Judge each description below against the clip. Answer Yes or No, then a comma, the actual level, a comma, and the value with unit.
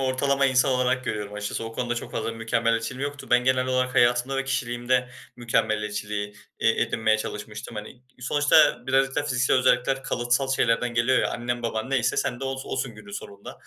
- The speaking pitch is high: No, low, 125 Hz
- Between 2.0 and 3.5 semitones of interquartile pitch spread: Yes, narrow, 2.5 semitones